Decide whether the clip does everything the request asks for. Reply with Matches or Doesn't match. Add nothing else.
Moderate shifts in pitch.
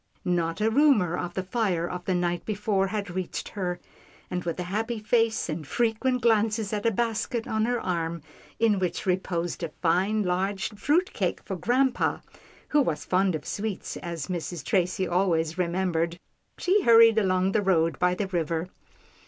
Matches